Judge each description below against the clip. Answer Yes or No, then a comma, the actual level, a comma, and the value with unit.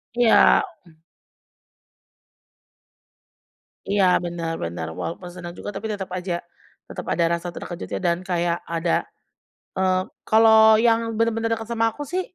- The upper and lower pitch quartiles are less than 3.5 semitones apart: No, average, 4.6 semitones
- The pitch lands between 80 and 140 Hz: No, high, 190 Hz